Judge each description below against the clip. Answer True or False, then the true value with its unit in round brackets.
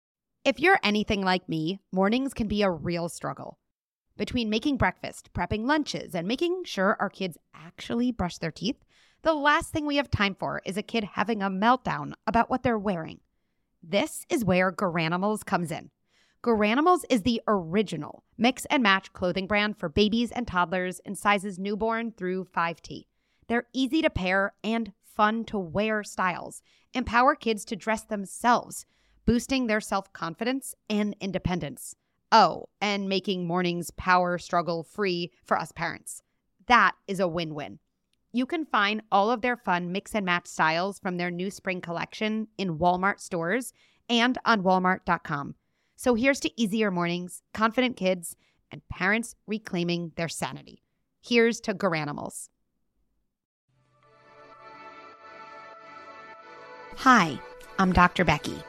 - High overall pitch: True (205 Hz)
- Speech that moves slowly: False (145 wpm)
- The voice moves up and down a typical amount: True (4.2 semitones)